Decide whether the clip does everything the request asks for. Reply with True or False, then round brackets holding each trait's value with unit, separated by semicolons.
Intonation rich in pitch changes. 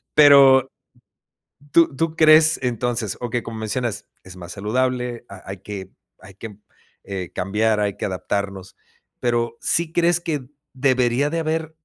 True (5.9 semitones)